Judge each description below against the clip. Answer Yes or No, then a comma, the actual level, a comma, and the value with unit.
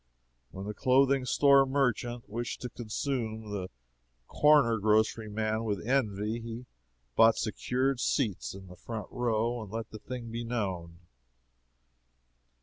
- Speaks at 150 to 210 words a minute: No, slow, 135 wpm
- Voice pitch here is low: Yes, low, 115 Hz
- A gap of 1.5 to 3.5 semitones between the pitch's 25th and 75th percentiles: Yes, average, 2.7 semitones